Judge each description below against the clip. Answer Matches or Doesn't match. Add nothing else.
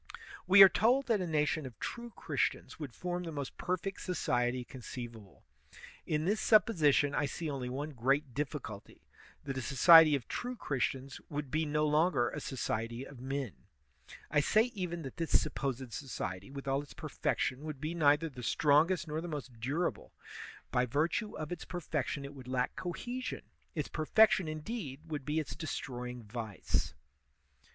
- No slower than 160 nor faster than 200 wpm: Matches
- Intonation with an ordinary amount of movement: Matches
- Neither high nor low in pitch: Matches